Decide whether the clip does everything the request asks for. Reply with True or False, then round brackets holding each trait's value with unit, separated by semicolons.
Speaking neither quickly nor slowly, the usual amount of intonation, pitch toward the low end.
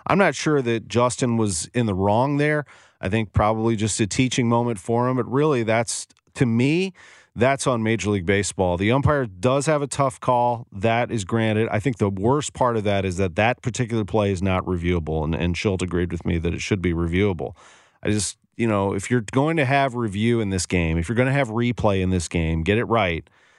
False (230 wpm; 4.2 semitones; 115 Hz)